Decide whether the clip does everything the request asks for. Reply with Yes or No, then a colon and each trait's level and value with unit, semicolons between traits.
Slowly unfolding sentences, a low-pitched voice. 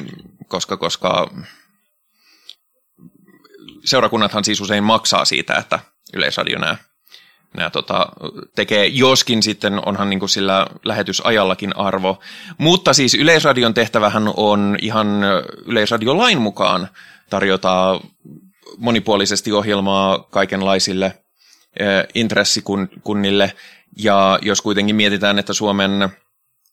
Yes: slow, 90 wpm; low, 100 Hz